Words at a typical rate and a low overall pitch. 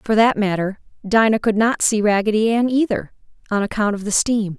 No: average, 195 wpm; high, 215 Hz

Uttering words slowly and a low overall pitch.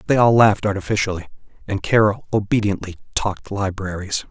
Yes: slow, 125 wpm; low, 100 Hz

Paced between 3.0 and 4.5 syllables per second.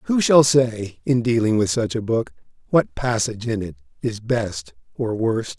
Yes: 4.3 syllables/s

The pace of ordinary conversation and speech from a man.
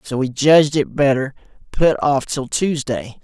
Yes: average, 165 wpm; male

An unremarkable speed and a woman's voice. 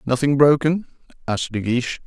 No: average, 145 wpm; male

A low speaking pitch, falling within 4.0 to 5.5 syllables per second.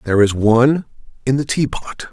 No: low, 125 Hz; 5.7 syllables/s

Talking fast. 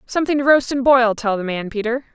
Yes: fast, 250 wpm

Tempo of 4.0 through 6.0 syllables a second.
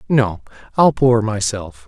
No: 3.7 syllables/s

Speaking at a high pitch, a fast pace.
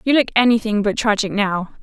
No: high, 215 Hz; average, 195 wpm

